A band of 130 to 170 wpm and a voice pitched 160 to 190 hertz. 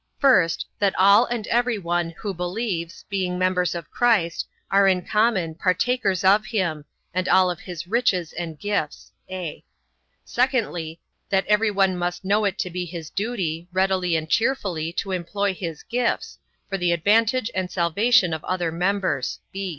Yes: average, 160 wpm; medium, 185 Hz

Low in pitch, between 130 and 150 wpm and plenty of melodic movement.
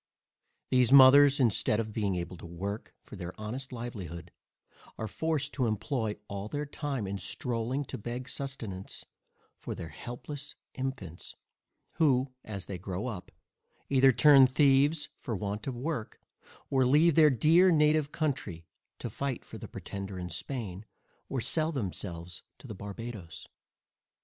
Yes: low, 120 Hz; average, 145 wpm; wide, 5.9 semitones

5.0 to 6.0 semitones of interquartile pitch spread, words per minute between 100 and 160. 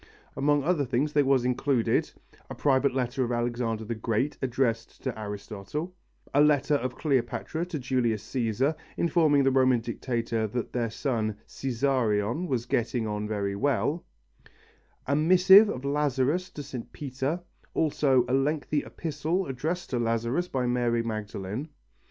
No: average, 4.0 semitones; average, 145 wpm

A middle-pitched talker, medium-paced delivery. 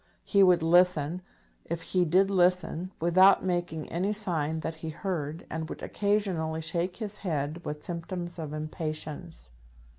Yes: medium, 170 Hz; average, 145 wpm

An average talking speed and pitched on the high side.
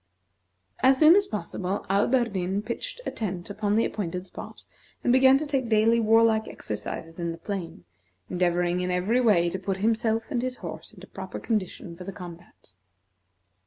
Yes: average, 165 wpm; high, 205 Hz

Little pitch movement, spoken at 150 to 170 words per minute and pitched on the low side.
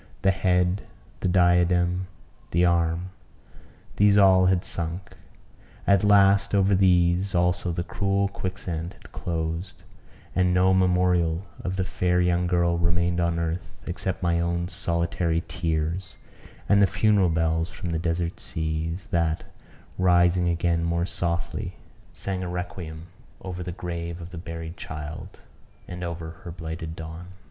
No: narrow, 1.7 semitones; average, 140 wpm; very low, 90 Hz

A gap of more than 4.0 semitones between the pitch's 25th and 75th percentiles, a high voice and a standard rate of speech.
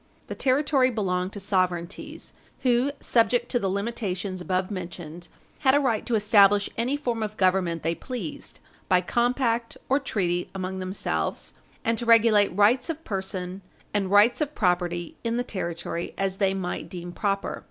Yes: average, 4.4 semitones; high, 200 Hz; average, 160 wpm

